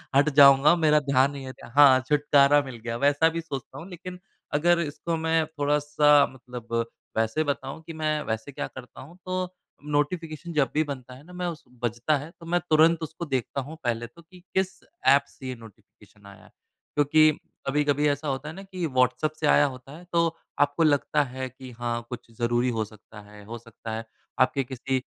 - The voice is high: No, medium, 145 Hz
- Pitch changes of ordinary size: Yes, average, 3.7 semitones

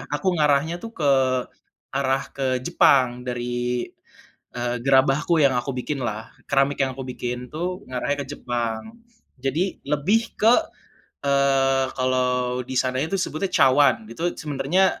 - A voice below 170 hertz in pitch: Yes, low, 135 Hz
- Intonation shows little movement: No, average, 3.0 semitones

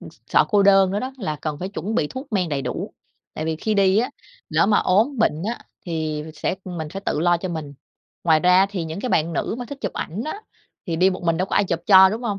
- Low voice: No, medium, 185 Hz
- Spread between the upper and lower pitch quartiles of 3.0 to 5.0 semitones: Yes, average, 4.2 semitones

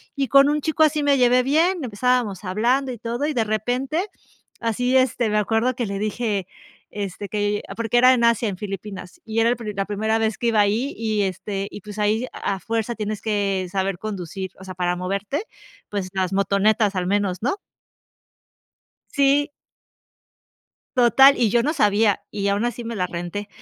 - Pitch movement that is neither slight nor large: Yes, average, 3.8 semitones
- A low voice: No, high, 215 Hz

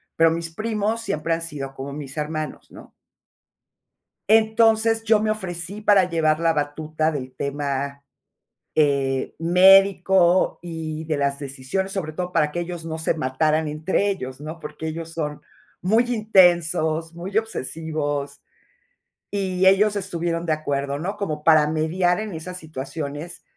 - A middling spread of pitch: Yes, average, 4.0 semitones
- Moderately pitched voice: Yes, medium, 165 Hz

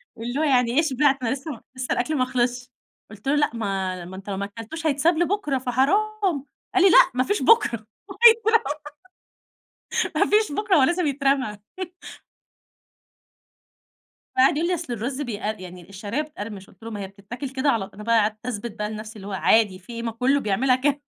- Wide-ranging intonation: Yes, wide, 5.8 semitones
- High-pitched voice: Yes, very high, 250 Hz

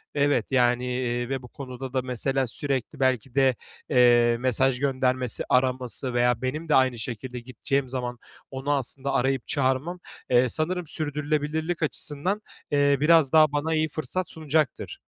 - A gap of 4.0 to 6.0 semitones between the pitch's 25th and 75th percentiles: No, average, 2.8 semitones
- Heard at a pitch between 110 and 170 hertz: Yes, low, 135 Hz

